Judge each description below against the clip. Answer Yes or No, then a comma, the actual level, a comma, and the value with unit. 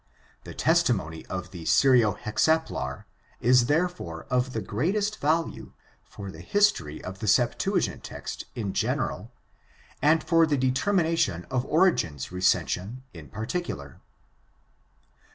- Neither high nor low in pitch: No, low, 125 Hz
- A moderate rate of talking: No, slow, 115 wpm